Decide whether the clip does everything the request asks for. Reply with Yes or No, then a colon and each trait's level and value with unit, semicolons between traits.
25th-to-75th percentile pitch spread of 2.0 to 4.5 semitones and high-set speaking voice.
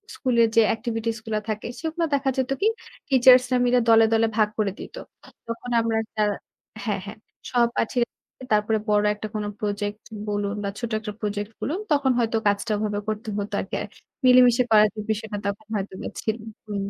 Yes: average, 2.8 semitones; high, 220 Hz